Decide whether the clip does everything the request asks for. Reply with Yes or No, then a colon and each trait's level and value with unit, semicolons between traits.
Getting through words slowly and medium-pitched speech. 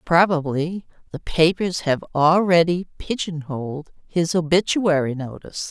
Yes: slow, 105 wpm; medium, 165 Hz